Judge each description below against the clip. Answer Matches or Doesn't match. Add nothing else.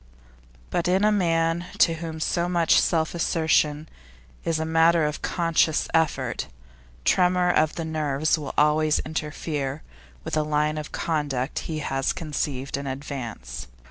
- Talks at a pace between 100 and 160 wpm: Matches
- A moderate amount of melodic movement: Doesn't match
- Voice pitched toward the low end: Doesn't match